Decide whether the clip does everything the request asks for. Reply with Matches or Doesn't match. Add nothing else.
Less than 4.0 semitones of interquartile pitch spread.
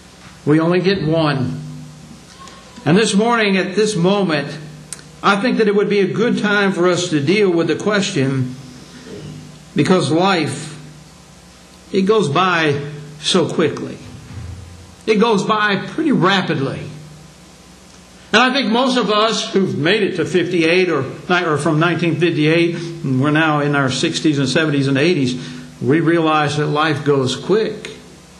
Doesn't match